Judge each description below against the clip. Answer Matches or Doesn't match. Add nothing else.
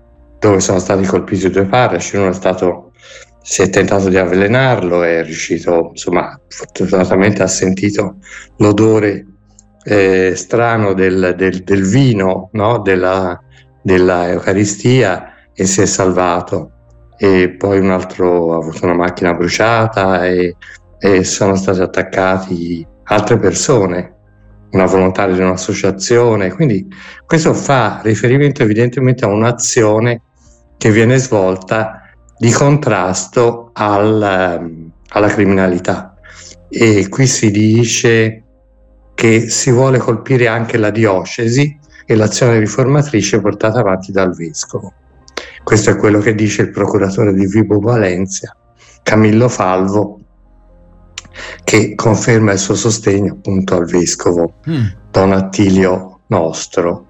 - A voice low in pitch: Matches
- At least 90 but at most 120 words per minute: Matches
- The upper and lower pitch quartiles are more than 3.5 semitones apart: Doesn't match